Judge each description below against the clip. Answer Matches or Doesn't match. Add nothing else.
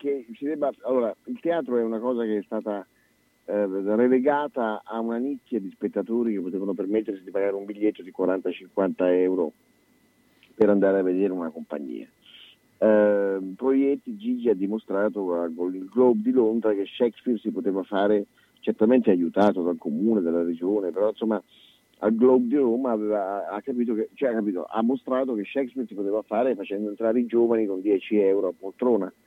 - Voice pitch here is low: Matches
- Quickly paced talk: Matches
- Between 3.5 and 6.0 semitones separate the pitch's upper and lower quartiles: Matches